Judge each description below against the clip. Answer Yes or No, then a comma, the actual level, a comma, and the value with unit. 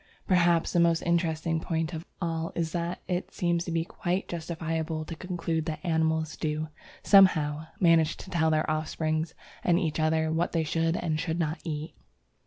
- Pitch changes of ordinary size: No, narrow, 1.4 semitones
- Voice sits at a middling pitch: Yes, medium, 165 Hz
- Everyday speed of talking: Yes, average, 175 wpm